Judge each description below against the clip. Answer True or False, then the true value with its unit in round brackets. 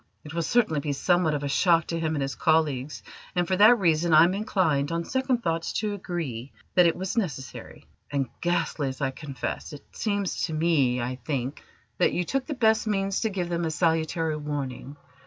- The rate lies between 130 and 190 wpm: False (205 wpm)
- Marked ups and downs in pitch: False (4.4 semitones)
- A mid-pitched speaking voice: True (165 Hz)